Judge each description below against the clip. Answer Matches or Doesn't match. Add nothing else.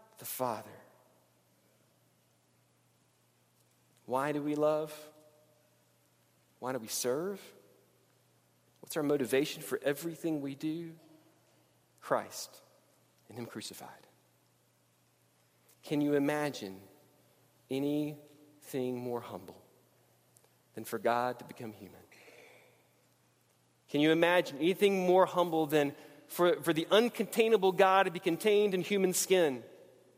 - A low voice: Doesn't match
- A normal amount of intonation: Doesn't match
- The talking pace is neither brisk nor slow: Doesn't match